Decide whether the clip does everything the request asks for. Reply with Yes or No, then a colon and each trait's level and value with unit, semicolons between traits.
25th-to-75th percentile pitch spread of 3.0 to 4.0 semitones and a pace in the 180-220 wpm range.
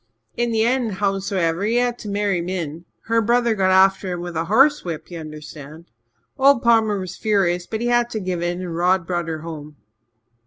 No: average, 4.7 semitones; average, 200 wpm